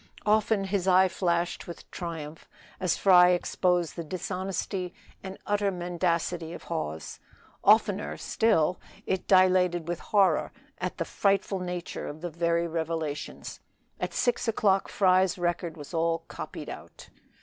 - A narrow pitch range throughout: Yes, narrow, 2.1 semitones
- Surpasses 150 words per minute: No, slow, 135 wpm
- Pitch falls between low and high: Yes, medium, 180 Hz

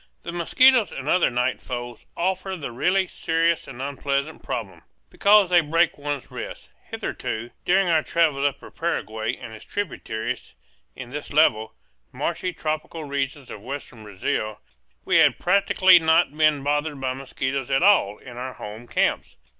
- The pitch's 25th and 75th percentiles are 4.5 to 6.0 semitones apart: Yes, wide, 5.5 semitones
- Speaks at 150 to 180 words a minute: Yes, average, 155 wpm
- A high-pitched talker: No, medium, 145 Hz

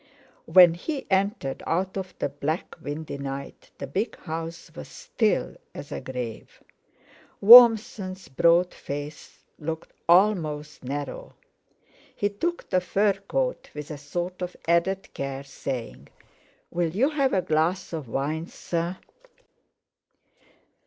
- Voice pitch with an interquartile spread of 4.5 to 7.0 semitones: Yes, average, 4.8 semitones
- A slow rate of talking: Yes, slow, 125 wpm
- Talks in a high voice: No, medium, 170 Hz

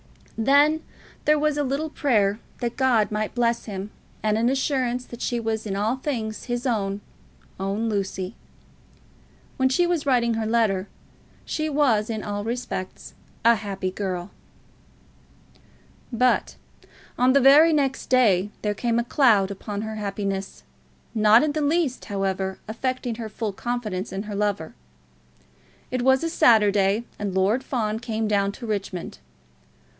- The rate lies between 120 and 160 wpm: Yes, average, 150 wpm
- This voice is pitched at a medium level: No, high, 225 Hz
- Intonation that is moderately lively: Yes, average, 4.0 semitones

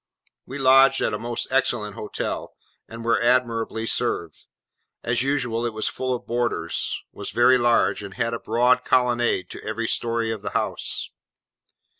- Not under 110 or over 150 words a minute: No, average, 160 wpm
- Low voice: Yes, low, 120 Hz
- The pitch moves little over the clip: Yes, narrow, 1.7 semitones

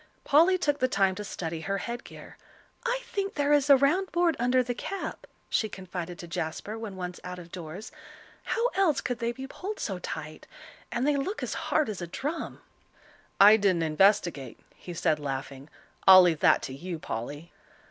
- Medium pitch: No, high, 200 Hz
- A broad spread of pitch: Yes, wide, 8.7 semitones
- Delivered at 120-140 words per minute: No, average, 185 wpm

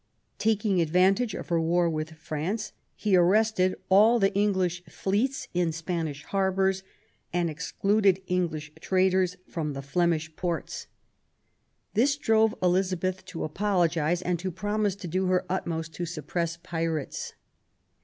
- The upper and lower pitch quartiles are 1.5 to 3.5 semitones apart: Yes, average, 2.9 semitones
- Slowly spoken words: Yes, slow, 130 wpm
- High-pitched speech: No, medium, 180 Hz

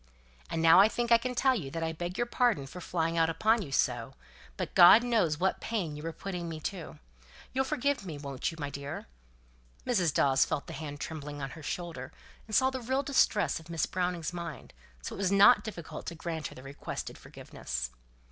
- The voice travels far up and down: Yes, wide, 6.2 semitones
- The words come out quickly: Yes, fast, 215 wpm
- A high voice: No, medium, 170 Hz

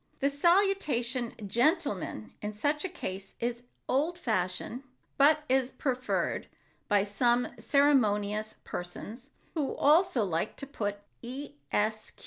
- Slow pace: Yes, slow, 110 wpm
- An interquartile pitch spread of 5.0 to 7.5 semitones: Yes, wide, 5.6 semitones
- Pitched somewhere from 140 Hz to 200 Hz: No, high, 245 Hz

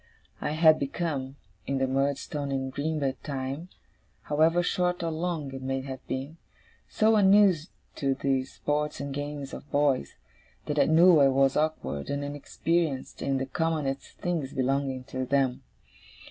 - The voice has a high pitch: No, medium, 140 Hz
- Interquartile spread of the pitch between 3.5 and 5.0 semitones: No, average, 2.9 semitones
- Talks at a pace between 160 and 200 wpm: No, average, 150 wpm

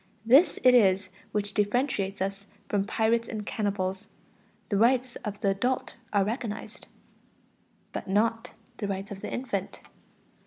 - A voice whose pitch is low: No, high, 210 Hz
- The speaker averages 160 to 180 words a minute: No, average, 140 wpm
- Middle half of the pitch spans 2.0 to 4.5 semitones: Yes, average, 2.8 semitones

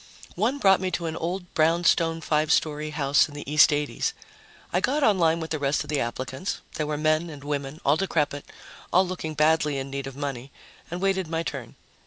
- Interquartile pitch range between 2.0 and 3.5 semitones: Yes, average, 3.0 semitones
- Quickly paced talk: Yes, fast, 210 wpm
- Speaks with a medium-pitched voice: Yes, medium, 155 Hz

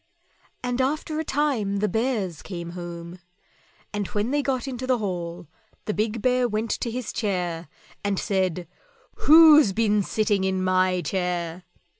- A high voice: Yes, high, 205 Hz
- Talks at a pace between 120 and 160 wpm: Yes, average, 150 wpm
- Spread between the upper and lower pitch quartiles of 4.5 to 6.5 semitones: Yes, average, 5.3 semitones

